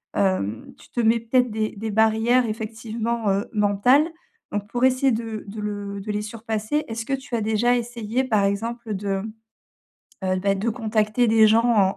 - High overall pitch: Yes, high, 220 Hz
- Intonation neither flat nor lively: No, narrow, 2.3 semitones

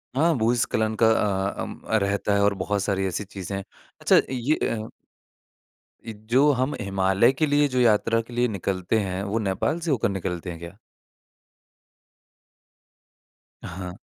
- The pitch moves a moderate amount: Yes, average, 3.8 semitones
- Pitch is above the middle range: No, low, 105 Hz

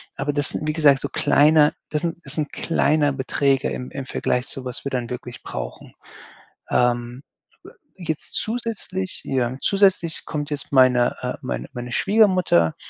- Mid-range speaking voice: Yes, medium, 145 Hz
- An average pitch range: Yes, average, 4.4 semitones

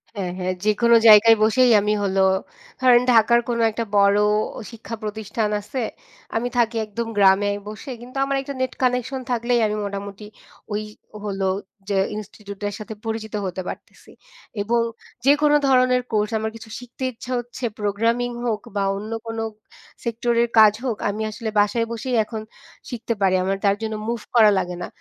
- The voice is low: No, high, 220 Hz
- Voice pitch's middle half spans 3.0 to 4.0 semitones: No, narrow, 2.6 semitones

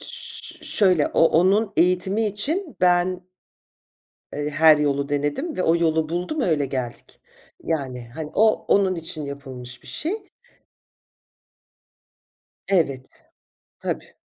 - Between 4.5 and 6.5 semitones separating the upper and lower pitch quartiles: Yes, average, 5.3 semitones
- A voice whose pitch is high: No, medium, 165 Hz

